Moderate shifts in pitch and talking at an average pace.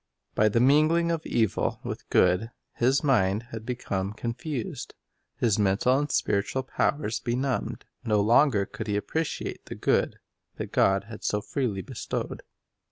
Yes: average, 4.6 semitones; average, 145 wpm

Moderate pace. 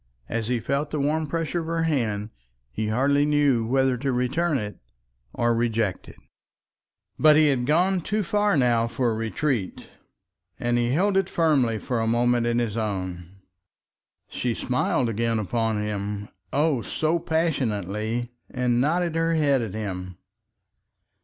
Yes: average, 155 wpm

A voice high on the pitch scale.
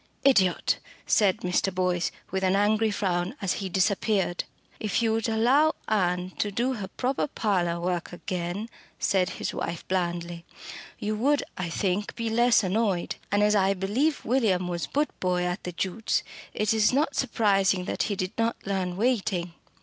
Yes: high, 195 Hz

